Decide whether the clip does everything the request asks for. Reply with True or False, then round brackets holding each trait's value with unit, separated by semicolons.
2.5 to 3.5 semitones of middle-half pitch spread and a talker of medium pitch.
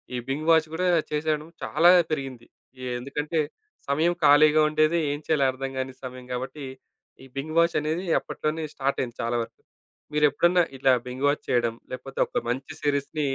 True (2.9 semitones; 145 Hz)